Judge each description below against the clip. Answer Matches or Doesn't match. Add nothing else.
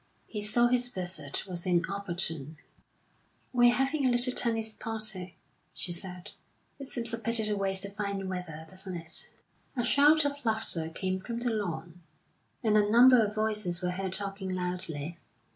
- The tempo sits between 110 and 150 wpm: Doesn't match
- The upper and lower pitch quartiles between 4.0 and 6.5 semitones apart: Matches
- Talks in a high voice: Matches